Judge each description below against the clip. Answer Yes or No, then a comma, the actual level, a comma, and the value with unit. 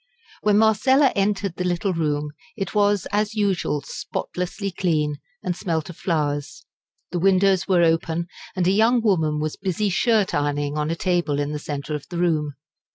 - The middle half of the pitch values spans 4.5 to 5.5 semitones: Yes, average, 4.8 semitones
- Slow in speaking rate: No, average, 170 wpm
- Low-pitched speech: No, medium, 175 Hz